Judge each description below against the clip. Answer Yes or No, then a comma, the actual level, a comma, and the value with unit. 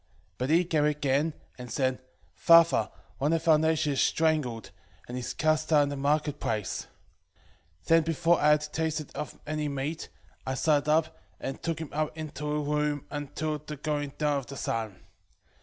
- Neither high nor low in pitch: Yes, medium, 150 Hz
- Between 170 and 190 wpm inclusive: Yes, average, 180 wpm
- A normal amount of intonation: No, narrow, 2.0 semitones